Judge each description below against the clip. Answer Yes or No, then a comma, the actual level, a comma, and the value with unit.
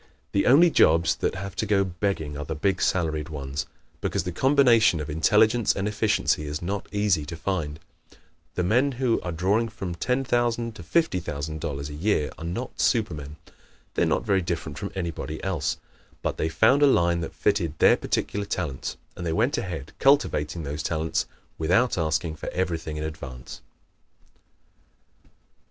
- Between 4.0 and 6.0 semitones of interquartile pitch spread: Yes, average, 5.3 semitones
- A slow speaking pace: No, average, 165 wpm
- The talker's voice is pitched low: Yes, very low, 90 Hz